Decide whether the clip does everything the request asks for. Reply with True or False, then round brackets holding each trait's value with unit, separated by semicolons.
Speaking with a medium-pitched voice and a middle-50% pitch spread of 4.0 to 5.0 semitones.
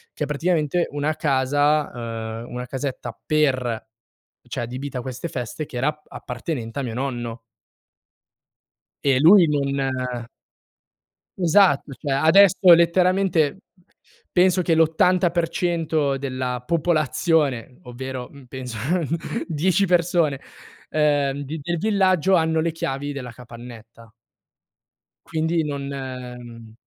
True (145 Hz; 4.6 semitones)